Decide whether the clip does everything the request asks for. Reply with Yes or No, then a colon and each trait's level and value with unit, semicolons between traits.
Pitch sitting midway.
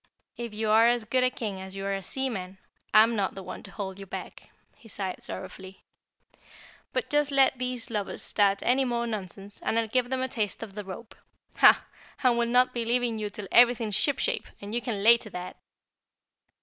No: high, 225 Hz